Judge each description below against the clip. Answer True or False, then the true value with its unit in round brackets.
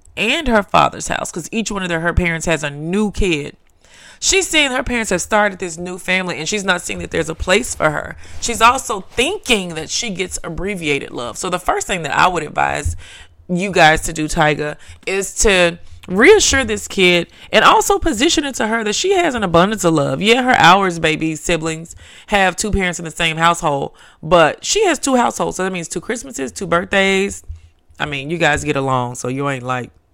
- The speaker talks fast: True (215 wpm)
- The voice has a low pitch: False (180 Hz)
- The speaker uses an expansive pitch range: True (5.7 semitones)